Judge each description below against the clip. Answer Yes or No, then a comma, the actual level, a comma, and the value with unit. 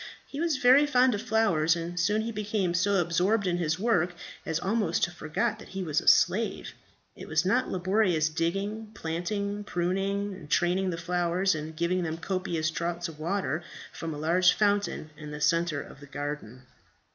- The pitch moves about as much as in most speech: Yes, average, 3.8 semitones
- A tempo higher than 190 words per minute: No, average, 180 wpm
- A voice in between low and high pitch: Yes, medium, 175 Hz